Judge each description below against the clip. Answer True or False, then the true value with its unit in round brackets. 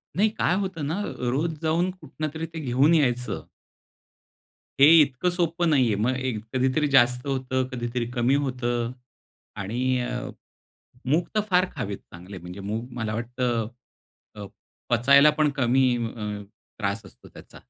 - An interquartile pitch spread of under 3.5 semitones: False (4.8 semitones)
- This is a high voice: False (130 Hz)